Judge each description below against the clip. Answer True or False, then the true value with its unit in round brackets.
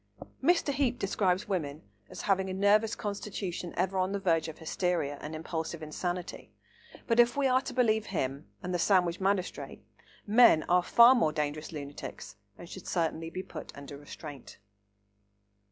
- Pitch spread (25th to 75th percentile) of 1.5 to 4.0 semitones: False (4.5 semitones)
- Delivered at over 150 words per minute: True (160 wpm)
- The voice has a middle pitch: True (180 Hz)